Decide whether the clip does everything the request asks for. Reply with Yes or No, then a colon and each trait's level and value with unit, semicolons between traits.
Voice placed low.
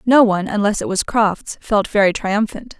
No: high, 210 Hz